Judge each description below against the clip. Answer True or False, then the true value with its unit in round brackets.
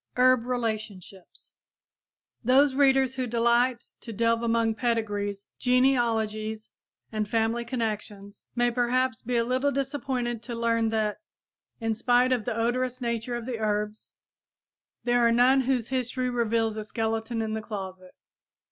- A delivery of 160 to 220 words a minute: False (140 wpm)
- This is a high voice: True (235 Hz)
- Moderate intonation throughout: False (2.2 semitones)